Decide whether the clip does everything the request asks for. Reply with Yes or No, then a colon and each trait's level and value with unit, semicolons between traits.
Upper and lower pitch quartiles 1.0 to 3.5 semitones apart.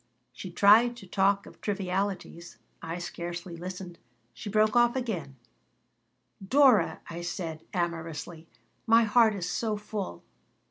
No: average, 4.0 semitones